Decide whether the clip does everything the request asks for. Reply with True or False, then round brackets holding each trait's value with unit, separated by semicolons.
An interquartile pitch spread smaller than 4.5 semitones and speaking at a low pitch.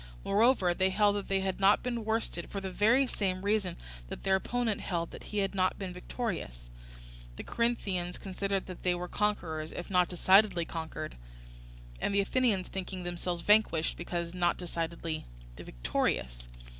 False (2.9 semitones; 185 Hz)